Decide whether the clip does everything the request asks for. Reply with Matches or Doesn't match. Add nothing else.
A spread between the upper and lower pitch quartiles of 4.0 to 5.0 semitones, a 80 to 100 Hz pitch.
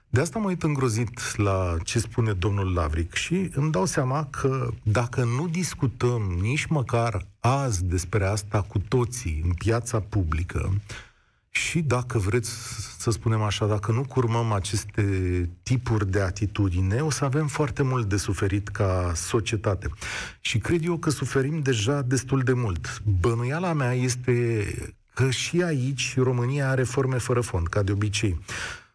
Doesn't match